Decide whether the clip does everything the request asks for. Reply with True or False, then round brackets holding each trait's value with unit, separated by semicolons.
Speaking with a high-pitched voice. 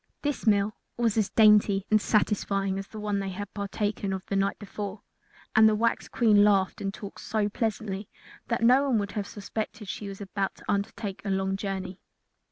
True (205 Hz)